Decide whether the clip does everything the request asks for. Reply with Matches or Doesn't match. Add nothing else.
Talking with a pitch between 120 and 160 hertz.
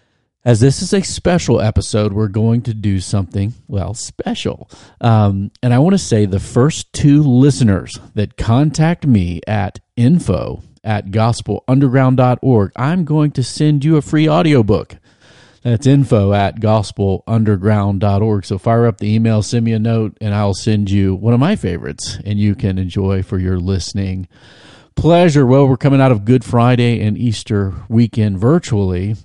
Doesn't match